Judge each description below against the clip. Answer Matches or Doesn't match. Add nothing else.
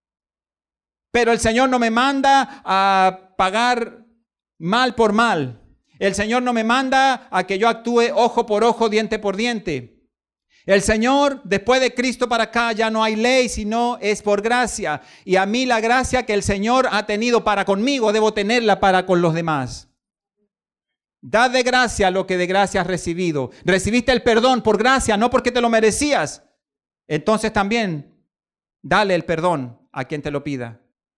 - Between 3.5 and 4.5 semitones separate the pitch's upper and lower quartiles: Matches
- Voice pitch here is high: Matches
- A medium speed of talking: Matches